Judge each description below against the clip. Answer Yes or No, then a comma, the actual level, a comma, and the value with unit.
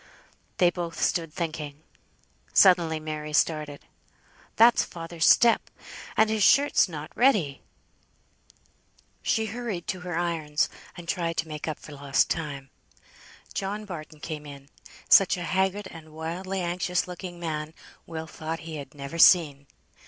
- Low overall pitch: No, medium, 165 Hz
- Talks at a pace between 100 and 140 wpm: Yes, slow, 135 wpm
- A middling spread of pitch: Yes, average, 3.1 semitones